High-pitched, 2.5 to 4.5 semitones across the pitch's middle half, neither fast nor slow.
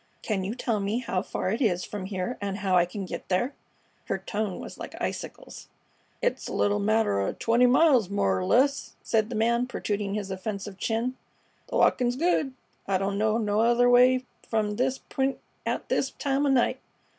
Yes: high, 220 Hz; average, 4.0 semitones; average, 190 wpm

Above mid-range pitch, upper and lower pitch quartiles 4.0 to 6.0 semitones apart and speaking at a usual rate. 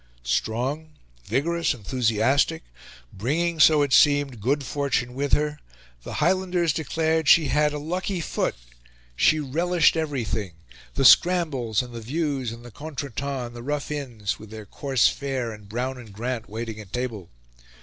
No: low, 135 Hz; average, 4.6 semitones; average, 150 wpm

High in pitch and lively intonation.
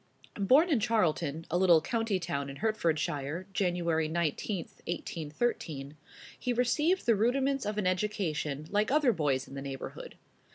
No: medium, 180 Hz; wide, 6.8 semitones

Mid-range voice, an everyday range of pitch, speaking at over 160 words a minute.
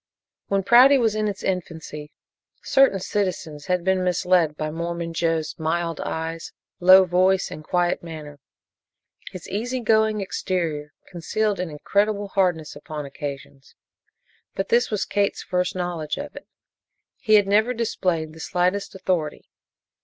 No: medium, 180 Hz; average, 3.9 semitones; average, 140 wpm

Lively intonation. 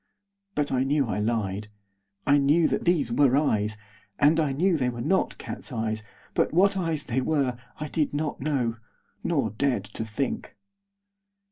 No: average, 4.7 semitones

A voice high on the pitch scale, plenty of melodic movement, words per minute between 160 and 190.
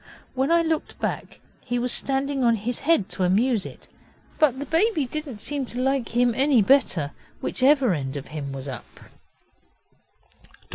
Yes: very high, 255 Hz; wide, 5.7 semitones; average, 165 wpm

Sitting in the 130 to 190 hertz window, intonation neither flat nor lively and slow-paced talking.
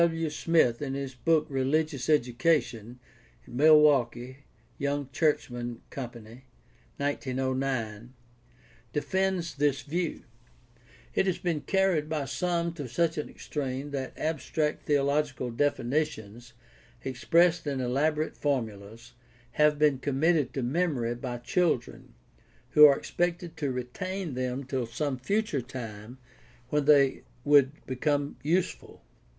Yes: medium, 140 Hz; average, 3.6 semitones; slow, 115 wpm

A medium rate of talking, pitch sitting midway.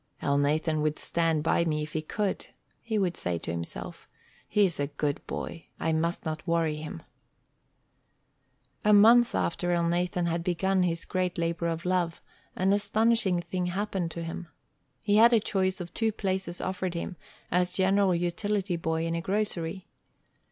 Yes: average, 160 wpm; medium, 175 Hz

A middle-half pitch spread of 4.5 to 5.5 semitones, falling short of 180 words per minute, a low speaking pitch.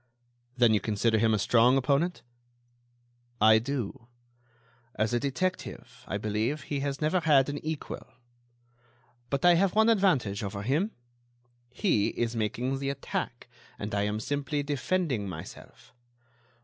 Yes: average, 5.1 semitones; slow, 135 wpm; low, 130 Hz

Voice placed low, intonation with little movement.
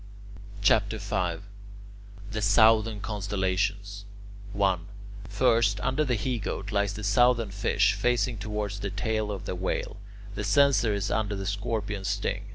Yes: low, 105 Hz; narrow, 1.9 semitones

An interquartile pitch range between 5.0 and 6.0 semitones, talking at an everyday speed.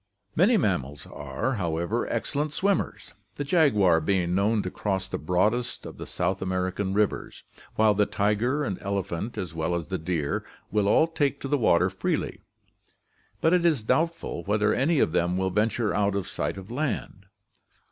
Yes: wide, 5.5 semitones; average, 170 wpm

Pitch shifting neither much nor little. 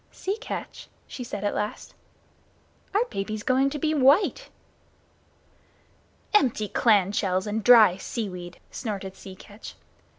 Yes: average, 5.0 semitones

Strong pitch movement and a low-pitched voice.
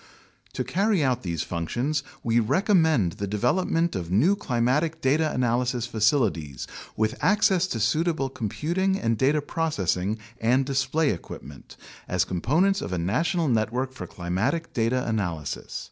Yes: wide, 7.3 semitones; low, 125 Hz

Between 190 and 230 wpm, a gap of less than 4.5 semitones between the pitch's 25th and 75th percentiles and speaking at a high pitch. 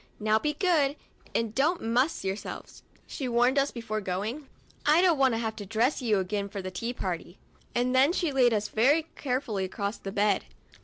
No: average, 200 wpm; average, 4.9 semitones; high, 235 Hz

